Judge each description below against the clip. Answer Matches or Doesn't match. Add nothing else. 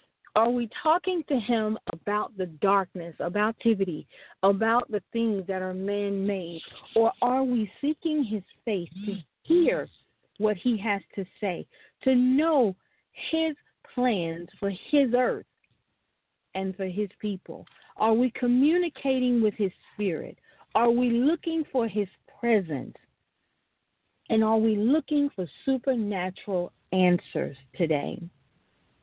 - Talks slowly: Matches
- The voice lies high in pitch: Matches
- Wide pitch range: Doesn't match